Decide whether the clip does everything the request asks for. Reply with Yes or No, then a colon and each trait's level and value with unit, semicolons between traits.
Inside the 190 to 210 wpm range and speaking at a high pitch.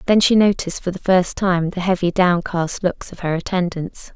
No: average, 200 wpm; medium, 180 Hz